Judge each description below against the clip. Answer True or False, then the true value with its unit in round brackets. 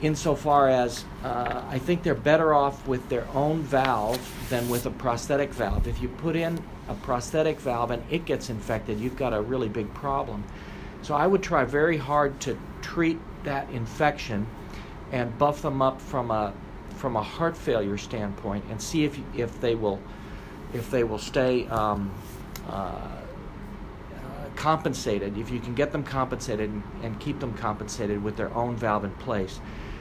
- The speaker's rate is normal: True (175 wpm)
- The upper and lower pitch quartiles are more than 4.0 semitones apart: True (5.3 semitones)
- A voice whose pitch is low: True (125 Hz)